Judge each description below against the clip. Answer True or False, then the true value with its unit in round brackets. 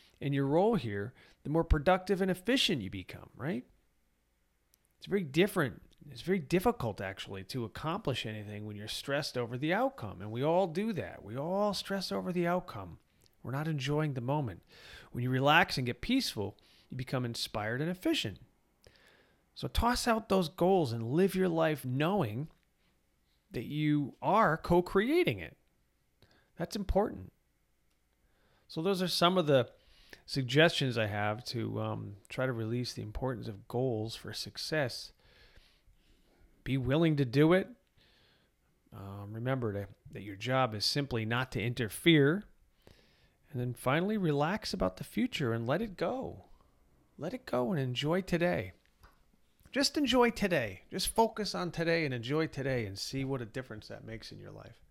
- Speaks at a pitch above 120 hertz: True (135 Hz)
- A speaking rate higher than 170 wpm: False (160 wpm)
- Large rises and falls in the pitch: True (8.0 semitones)